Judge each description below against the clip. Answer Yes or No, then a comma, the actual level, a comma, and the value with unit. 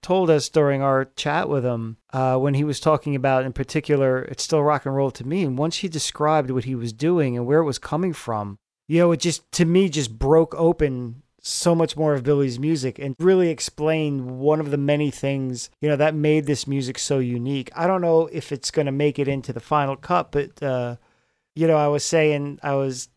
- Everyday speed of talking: No, fast, 230 wpm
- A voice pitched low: No, medium, 145 Hz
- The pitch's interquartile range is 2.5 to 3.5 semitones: Yes, average, 2.9 semitones